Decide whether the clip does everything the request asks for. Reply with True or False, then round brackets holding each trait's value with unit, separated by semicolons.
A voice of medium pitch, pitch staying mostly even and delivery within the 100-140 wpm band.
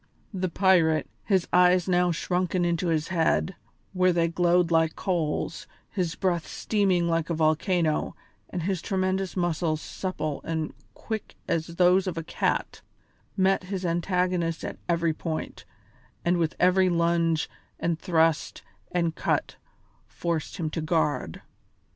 True (170 Hz; 2.0 semitones; 135 wpm)